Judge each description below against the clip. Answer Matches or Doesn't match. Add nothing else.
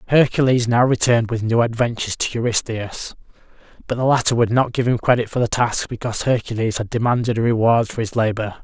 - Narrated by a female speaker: Doesn't match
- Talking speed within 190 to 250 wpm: Matches